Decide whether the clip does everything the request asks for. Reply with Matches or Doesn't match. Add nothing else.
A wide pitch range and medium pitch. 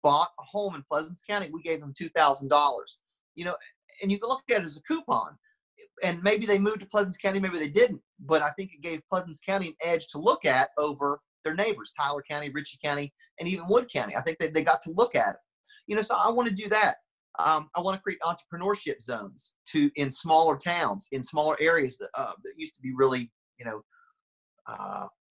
Matches